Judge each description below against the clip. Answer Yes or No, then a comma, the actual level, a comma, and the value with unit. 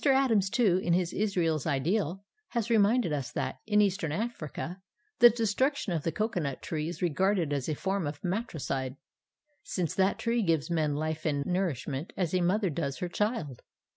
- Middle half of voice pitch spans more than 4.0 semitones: Yes, average, 5.3 semitones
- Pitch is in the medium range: Yes, medium, 180 Hz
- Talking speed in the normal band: Yes, average, 170 wpm